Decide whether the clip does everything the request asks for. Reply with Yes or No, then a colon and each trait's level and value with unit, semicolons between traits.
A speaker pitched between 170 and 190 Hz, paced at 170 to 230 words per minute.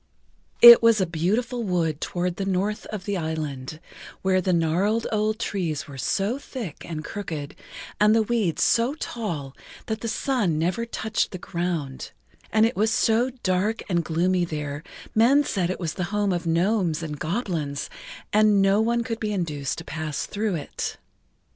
Yes: medium, 185 Hz; average, 175 wpm